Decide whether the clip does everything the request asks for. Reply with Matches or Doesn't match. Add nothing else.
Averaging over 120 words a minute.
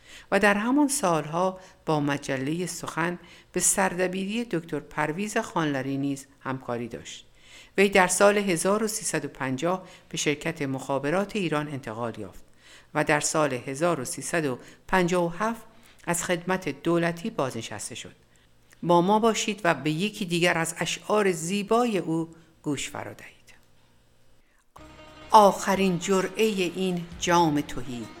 Doesn't match